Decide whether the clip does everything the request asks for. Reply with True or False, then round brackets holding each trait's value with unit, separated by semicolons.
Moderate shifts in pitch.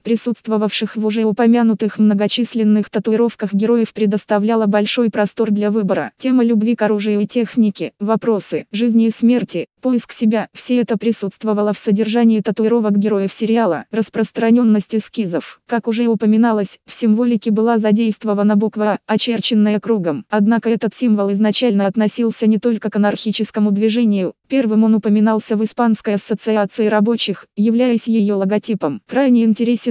False (1.6 semitones)